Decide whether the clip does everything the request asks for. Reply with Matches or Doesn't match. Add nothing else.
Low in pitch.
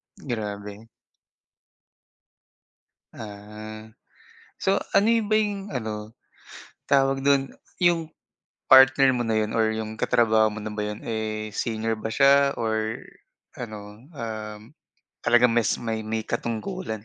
Matches